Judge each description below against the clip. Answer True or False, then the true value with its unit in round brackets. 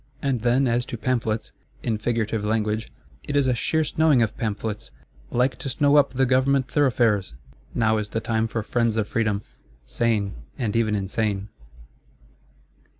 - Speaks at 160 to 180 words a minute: False (150 wpm)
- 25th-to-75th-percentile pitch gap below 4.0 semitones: True (3.0 semitones)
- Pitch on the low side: True (115 Hz)